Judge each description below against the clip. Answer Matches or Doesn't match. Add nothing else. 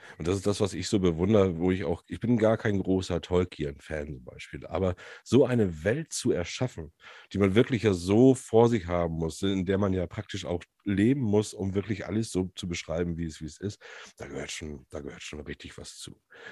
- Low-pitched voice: Matches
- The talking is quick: Matches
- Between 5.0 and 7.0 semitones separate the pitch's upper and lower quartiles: Doesn't match